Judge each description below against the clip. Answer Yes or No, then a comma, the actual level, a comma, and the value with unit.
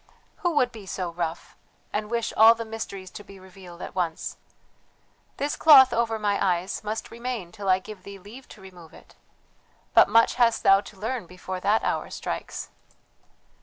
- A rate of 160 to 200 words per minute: Yes, average, 175 wpm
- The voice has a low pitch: No, high, 205 Hz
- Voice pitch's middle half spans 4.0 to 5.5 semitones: No, average, 3.6 semitones